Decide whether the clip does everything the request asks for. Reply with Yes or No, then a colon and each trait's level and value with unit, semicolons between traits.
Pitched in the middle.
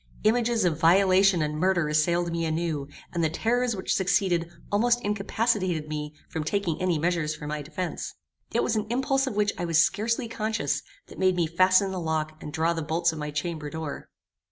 Yes: medium, 175 Hz